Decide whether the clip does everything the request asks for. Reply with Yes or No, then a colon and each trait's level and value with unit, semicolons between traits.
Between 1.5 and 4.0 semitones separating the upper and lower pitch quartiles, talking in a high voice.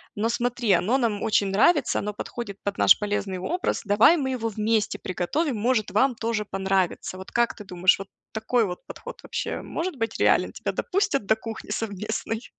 Yes: average, 3.5 semitones; high, 220 Hz